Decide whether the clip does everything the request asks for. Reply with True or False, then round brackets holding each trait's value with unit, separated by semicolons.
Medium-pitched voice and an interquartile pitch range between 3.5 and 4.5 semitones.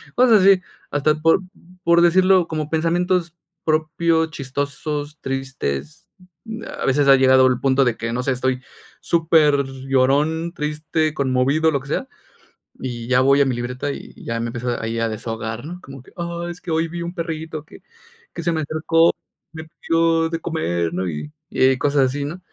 True (150 Hz; 4.0 semitones)